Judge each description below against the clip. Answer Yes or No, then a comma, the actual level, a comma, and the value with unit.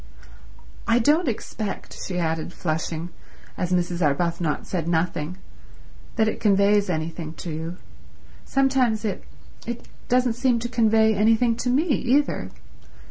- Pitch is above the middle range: Yes, high, 205 Hz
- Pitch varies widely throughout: Yes, wide, 5.9 semitones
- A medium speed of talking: No, slow, 125 wpm